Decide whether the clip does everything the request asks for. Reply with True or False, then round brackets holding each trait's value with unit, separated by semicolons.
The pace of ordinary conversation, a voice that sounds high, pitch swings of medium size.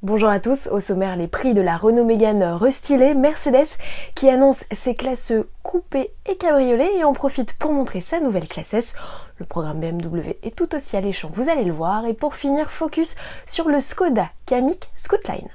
False (190 wpm; 255 Hz; 6.4 semitones)